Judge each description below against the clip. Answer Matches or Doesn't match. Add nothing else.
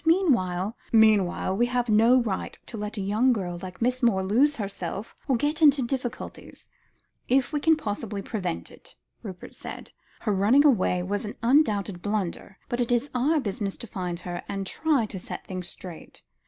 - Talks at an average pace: Matches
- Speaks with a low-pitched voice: Doesn't match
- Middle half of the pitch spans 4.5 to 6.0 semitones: Matches